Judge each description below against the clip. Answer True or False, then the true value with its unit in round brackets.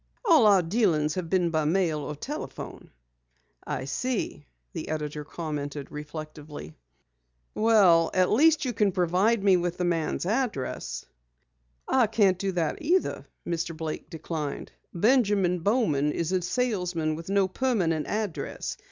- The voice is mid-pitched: True (180 Hz)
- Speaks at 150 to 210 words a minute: False (135 wpm)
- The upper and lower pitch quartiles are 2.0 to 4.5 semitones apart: False (5.2 semitones)